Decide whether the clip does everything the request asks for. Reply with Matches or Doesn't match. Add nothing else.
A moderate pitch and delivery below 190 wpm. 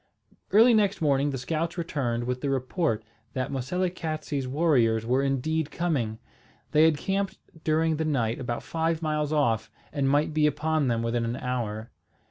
Matches